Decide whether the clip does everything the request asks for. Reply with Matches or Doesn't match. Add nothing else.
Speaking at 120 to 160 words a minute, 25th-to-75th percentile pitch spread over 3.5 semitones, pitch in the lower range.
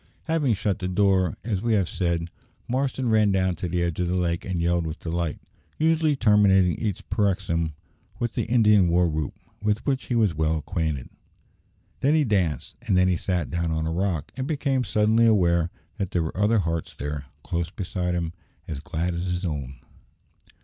Doesn't match